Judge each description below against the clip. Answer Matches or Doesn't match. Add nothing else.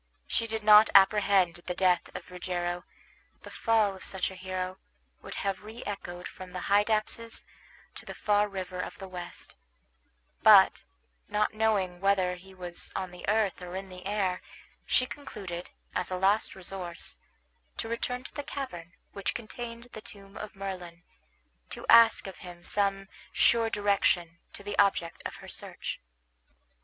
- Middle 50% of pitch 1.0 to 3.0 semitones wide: Matches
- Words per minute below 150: Doesn't match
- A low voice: Doesn't match